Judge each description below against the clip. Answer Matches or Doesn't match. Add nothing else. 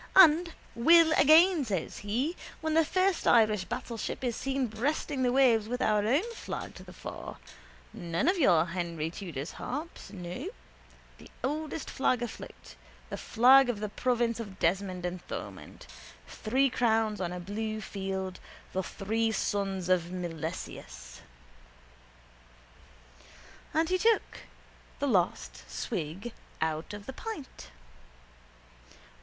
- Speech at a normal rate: Doesn't match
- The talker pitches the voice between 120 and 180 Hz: Doesn't match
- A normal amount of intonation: Doesn't match